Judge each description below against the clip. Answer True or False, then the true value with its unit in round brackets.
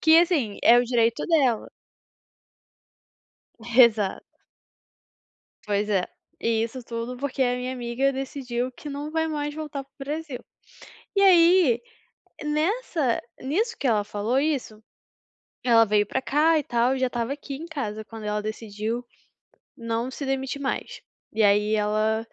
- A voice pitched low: False (250 Hz)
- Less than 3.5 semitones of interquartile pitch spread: False (4.6 semitones)